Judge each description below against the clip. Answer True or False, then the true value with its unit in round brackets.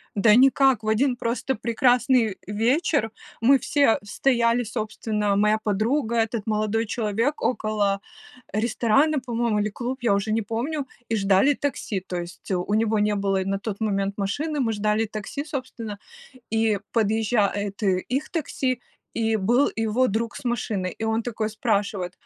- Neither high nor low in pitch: False (220 Hz)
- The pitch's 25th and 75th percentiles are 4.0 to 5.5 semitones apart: False (2.9 semitones)